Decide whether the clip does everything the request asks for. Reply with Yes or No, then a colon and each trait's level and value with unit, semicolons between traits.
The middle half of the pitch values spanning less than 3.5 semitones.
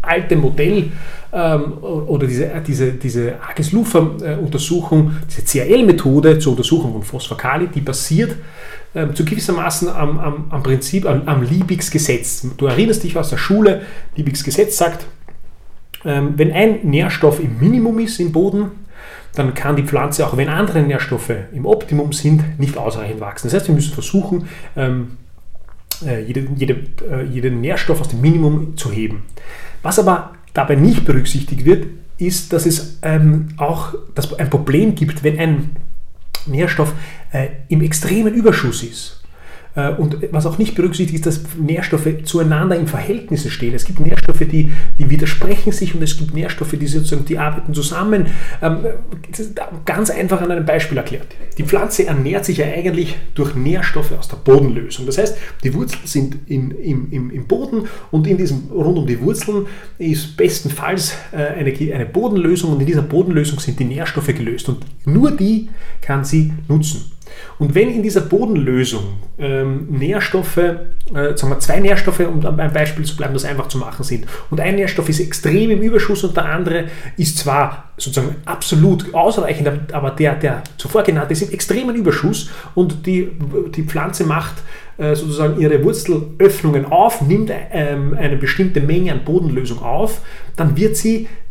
No: average, 3.8 semitones